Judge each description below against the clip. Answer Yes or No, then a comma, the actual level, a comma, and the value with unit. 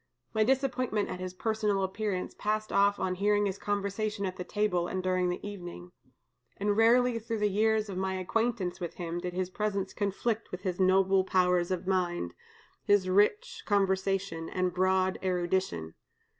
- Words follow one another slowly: No, average, 165 wpm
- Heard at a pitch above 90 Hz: Yes, high, 190 Hz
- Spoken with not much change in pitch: Yes, narrow, 2.3 semitones